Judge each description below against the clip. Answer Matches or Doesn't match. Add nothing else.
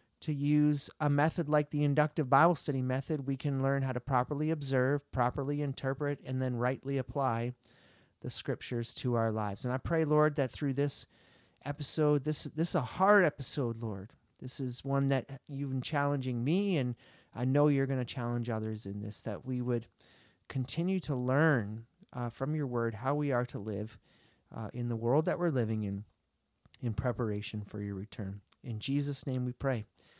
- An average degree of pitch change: Matches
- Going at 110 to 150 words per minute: Doesn't match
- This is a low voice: Matches